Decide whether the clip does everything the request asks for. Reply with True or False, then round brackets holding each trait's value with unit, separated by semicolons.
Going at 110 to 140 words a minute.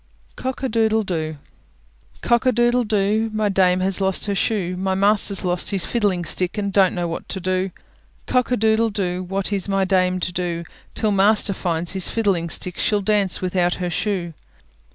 False (190 wpm)